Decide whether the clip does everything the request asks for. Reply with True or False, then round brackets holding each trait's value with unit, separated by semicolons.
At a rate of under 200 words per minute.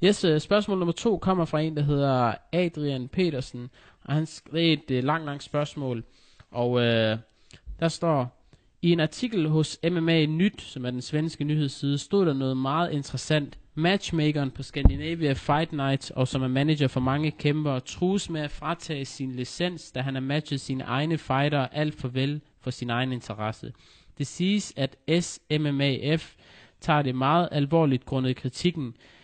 True (165 wpm)